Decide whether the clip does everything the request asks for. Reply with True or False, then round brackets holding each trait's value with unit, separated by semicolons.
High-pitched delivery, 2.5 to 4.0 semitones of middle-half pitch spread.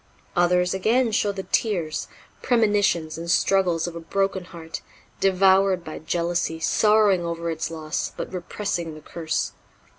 False (175 Hz; 2.9 semitones)